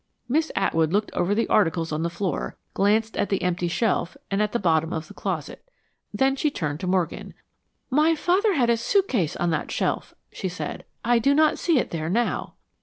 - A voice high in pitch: Yes, high, 200 Hz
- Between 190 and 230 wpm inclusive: Yes, average, 200 wpm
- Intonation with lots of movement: Yes, wide, 7.0 semitones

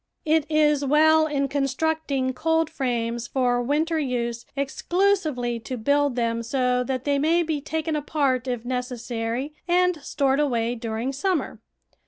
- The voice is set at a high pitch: Yes, very high, 275 Hz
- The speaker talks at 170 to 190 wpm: No, slow, 135 wpm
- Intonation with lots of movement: No, average, 4.0 semitones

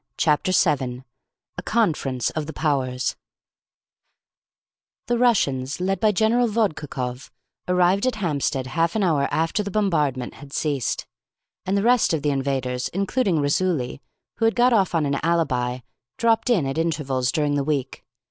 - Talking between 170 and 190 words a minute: No, average, 150 wpm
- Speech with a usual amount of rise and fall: No, wide, 6.5 semitones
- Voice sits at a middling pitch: Yes, medium, 155 Hz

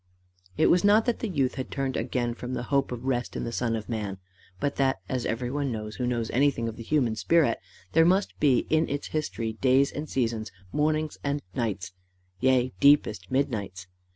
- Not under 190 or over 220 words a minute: Yes, average, 195 wpm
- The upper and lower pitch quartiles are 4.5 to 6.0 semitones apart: No, average, 3.8 semitones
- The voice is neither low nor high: No, low, 130 Hz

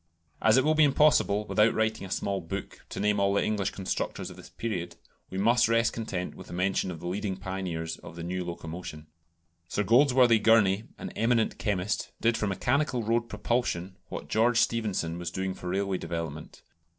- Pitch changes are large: No, average, 4.0 semitones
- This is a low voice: Yes, low, 100 Hz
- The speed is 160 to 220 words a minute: Yes, average, 185 wpm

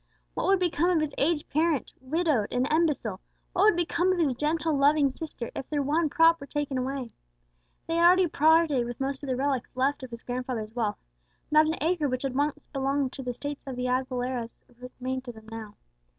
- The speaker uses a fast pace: Yes, fast, 210 wpm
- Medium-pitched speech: No, very high, 280 Hz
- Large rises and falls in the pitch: No, average, 3.9 semitones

